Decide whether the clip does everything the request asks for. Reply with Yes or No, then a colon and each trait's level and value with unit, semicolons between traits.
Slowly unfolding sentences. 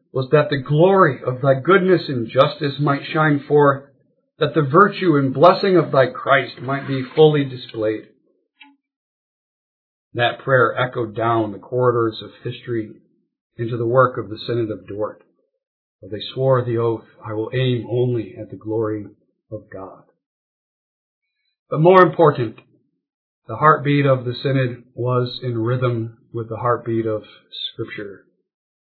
No: average, 145 wpm